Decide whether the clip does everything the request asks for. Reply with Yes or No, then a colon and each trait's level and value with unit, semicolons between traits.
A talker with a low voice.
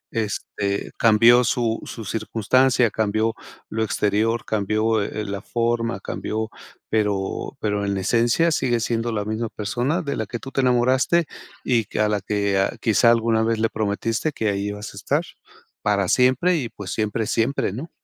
Yes: low, 110 Hz